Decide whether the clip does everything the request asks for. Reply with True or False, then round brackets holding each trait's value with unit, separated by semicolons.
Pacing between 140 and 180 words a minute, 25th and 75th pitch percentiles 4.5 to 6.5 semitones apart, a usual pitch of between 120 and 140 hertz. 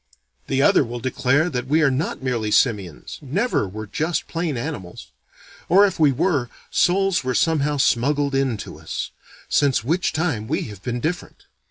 True (170 wpm; 5.0 semitones; 135 Hz)